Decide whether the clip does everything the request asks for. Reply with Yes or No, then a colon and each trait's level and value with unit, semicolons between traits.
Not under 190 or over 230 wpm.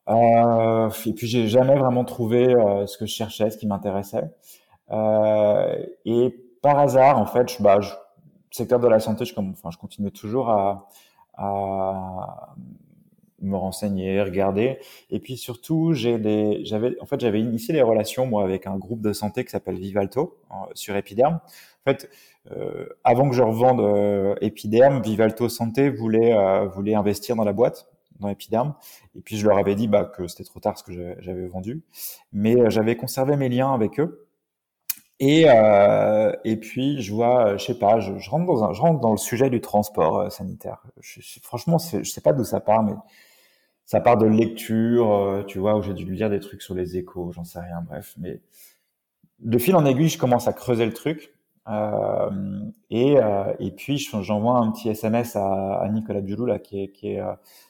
Yes: average, 195 wpm